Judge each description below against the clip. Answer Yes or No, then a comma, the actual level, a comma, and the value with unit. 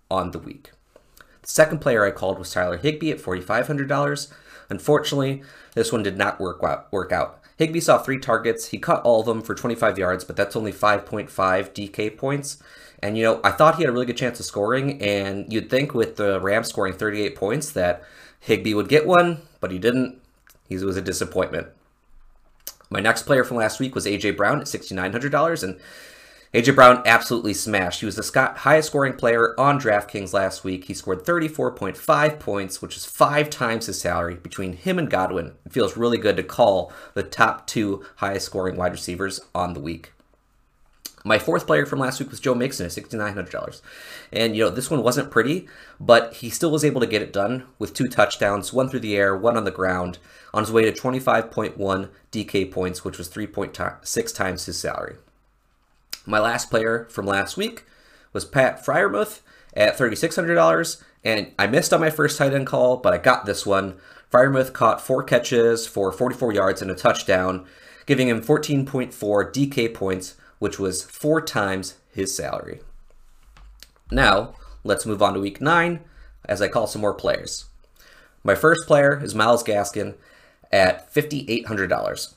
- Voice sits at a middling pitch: No, low, 115 Hz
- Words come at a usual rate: Yes, average, 180 wpm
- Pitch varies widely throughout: Yes, wide, 5.7 semitones